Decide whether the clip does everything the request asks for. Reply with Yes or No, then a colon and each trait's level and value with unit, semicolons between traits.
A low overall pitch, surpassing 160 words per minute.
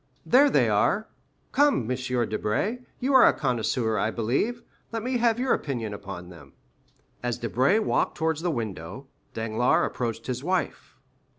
No: low, 125 Hz; average, 155 wpm